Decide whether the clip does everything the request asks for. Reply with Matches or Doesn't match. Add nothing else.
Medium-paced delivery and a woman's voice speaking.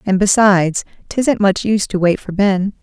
Matches